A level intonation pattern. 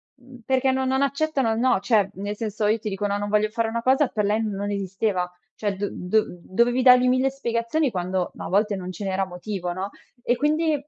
No: average, 4.4 semitones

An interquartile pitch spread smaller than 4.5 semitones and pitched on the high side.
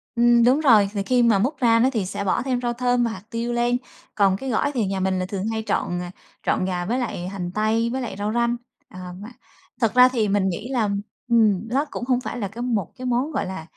Yes: average, 3.8 semitones; high, 230 Hz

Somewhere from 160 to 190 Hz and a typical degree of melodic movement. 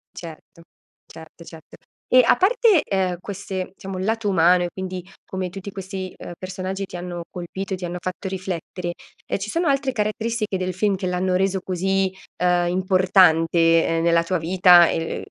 No: medium, 185 Hz; narrow, 1.7 semitones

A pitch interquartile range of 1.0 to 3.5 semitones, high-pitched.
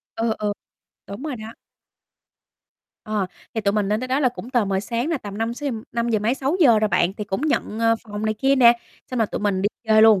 Yes: average, 3.2 semitones; high, 225 Hz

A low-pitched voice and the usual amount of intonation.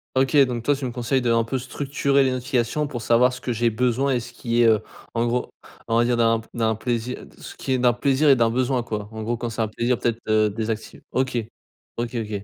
No: low, 120 Hz; narrow, 2.0 semitones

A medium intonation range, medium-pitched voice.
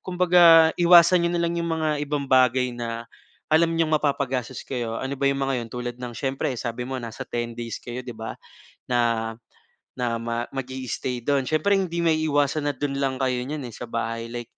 No: average, 4.6 semitones; low, 130 Hz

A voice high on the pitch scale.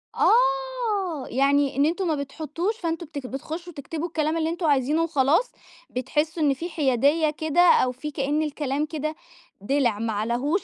Yes: very high, 305 Hz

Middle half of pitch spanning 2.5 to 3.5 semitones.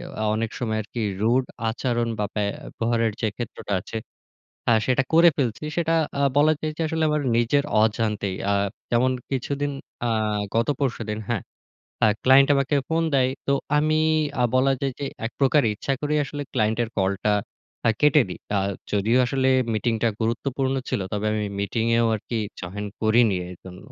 No: average, 4.1 semitones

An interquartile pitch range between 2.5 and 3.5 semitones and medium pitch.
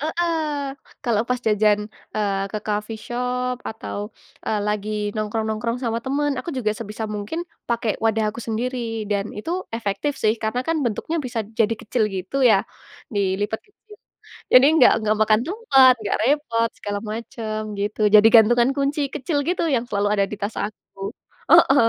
No: average, 3.2 semitones; high, 225 Hz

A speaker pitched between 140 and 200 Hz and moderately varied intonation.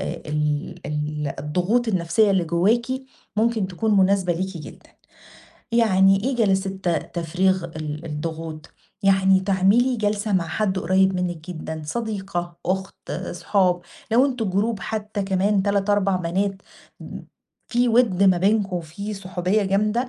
Yes: high, 190 Hz; average, 3.1 semitones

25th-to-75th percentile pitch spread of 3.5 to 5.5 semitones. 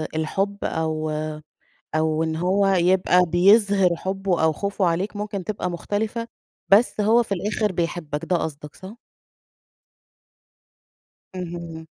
Yes: average, 3.8 semitones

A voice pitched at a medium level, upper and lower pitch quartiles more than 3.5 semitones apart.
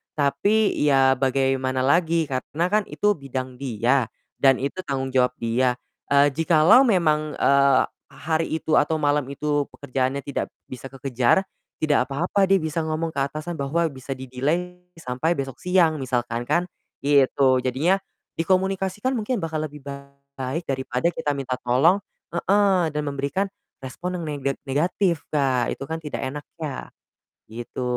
Yes: medium, 145 Hz; average, 3.9 semitones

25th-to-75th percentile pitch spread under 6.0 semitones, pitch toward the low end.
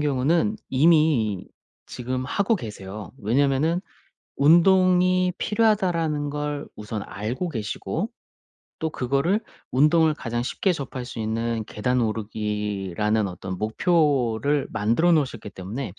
No: wide, 6.9 semitones; low, 130 Hz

